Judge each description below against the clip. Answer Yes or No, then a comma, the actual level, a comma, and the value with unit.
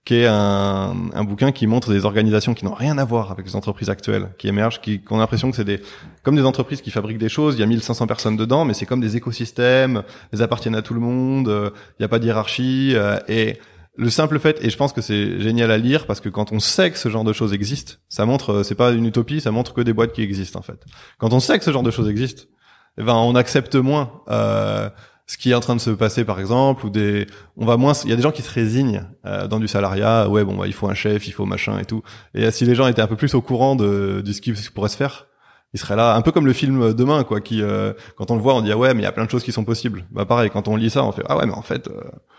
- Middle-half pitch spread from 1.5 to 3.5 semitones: Yes, average, 3.0 semitones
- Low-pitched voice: Yes, low, 115 Hz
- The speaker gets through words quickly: Yes, fast, 300 wpm